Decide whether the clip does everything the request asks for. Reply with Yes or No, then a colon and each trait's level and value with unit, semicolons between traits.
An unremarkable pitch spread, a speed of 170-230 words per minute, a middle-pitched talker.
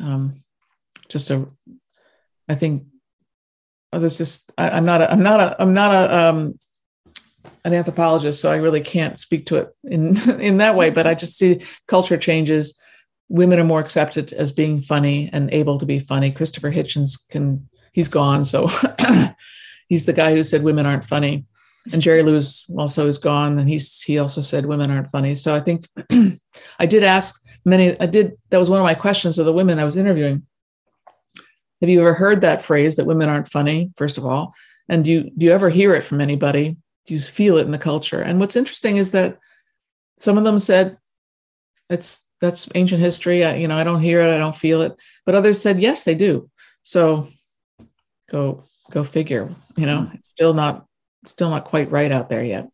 Yes: average, 3.4 semitones; average, 200 wpm; medium, 160 Hz